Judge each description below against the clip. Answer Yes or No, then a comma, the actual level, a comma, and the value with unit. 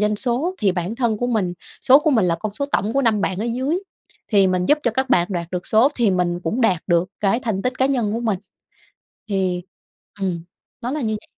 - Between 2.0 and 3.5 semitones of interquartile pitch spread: No, average, 5.2 semitones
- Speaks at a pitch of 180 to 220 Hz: Yes, high, 215 Hz